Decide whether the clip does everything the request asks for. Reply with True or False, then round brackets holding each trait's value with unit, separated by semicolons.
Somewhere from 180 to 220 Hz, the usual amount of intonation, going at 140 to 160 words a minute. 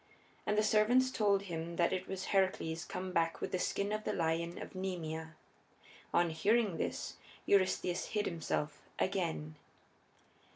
True (185 Hz; 3.4 semitones; 150 wpm)